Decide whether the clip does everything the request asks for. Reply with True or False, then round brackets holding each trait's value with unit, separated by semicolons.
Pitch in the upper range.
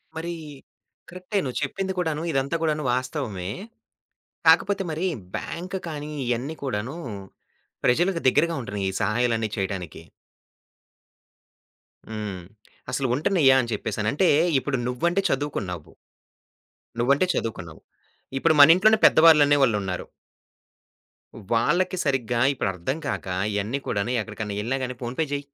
False (135 Hz)